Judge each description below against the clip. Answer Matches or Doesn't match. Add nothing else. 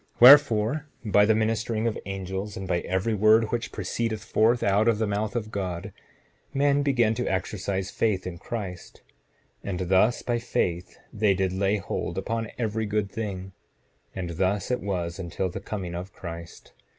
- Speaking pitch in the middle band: Doesn't match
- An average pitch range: Matches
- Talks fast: Doesn't match